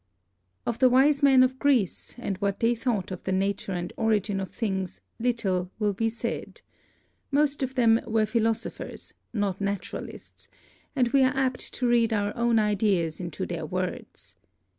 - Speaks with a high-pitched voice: Yes, high, 225 Hz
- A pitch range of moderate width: Yes, average, 4.0 semitones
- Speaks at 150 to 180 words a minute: Yes, average, 160 wpm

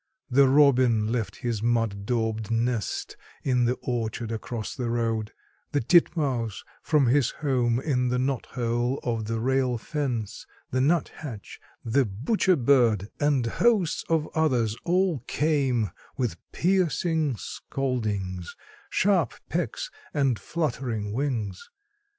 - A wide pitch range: No, average, 4.1 semitones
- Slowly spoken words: Yes, slow, 120 wpm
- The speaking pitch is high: No, low, 125 Hz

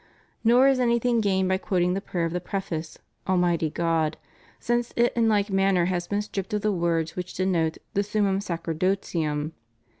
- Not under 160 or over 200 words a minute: Yes, average, 175 wpm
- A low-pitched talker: No, high, 190 Hz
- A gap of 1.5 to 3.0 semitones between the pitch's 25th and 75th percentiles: No, average, 3.5 semitones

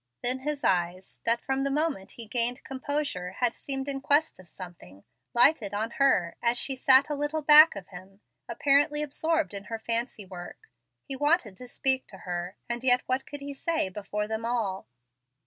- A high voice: Yes, high, 245 Hz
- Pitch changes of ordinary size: No, wide, 6.1 semitones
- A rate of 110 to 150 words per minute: No, average, 185 wpm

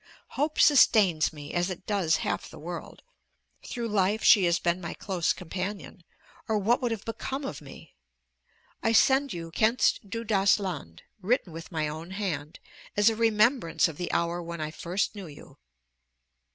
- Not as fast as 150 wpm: No, average, 170 wpm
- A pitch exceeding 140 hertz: Yes, high, 190 Hz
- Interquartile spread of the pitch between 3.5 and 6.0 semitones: Yes, average, 4.7 semitones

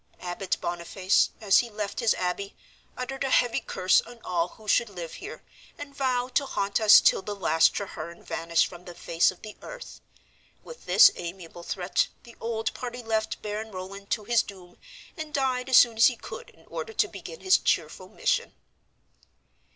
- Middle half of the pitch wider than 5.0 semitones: Yes, wide, 5.4 semitones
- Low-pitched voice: No, high, 210 Hz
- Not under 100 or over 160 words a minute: No, average, 180 wpm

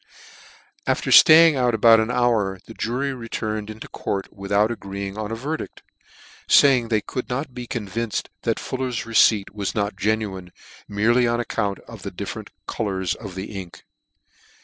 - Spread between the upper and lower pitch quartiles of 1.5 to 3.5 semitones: Yes, average, 3.2 semitones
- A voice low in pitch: Yes, low, 110 Hz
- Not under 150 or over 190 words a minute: Yes, average, 160 wpm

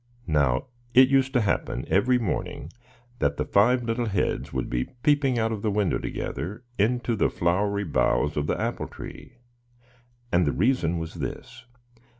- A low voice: Yes, low, 105 Hz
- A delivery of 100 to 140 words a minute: No, average, 160 wpm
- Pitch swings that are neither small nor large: No, wide, 6.6 semitones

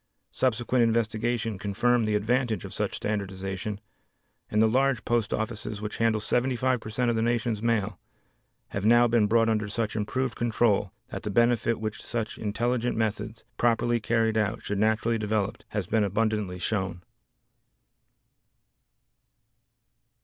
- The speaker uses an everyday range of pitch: No, narrow, 2.0 semitones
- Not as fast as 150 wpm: Yes, average, 140 wpm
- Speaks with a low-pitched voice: Yes, low, 110 Hz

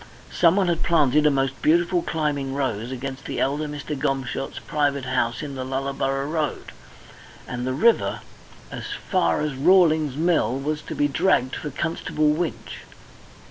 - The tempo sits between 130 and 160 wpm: Yes, average, 150 wpm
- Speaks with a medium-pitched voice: Yes, medium, 145 Hz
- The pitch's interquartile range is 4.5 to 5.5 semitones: No, average, 2.8 semitones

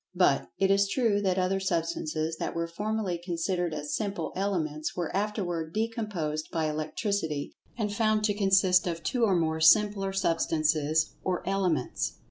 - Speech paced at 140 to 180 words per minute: Yes, average, 150 wpm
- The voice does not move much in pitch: No, average, 4.0 semitones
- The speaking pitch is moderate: Yes, medium, 180 Hz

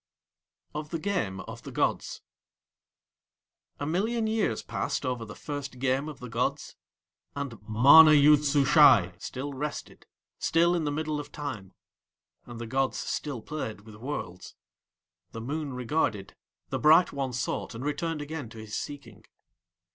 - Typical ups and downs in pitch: Yes, average, 4.5 semitones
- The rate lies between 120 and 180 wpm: Yes, average, 150 wpm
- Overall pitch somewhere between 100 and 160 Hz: Yes, medium, 140 Hz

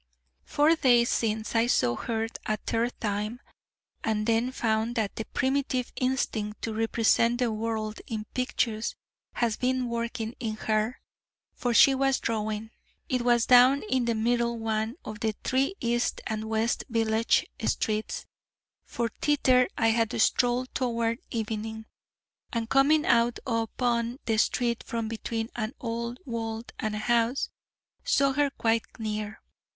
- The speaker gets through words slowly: No, average, 145 wpm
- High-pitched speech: Yes, high, 230 Hz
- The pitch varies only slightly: Yes, narrow, 1.9 semitones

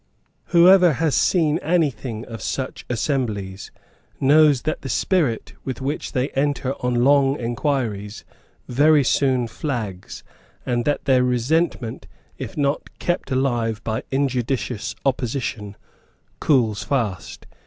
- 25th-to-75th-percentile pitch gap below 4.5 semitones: Yes, average, 3.8 semitones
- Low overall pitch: Yes, low, 130 Hz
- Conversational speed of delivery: No, slow, 115 wpm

